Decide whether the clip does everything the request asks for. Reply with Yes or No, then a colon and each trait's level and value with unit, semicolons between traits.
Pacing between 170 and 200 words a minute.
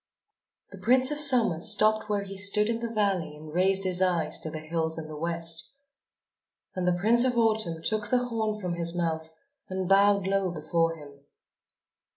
Yes: average, 185 wpm